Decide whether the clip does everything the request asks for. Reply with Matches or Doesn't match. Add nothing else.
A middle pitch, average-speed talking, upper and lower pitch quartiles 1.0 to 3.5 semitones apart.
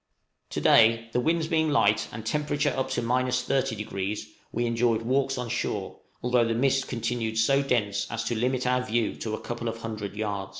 Doesn't match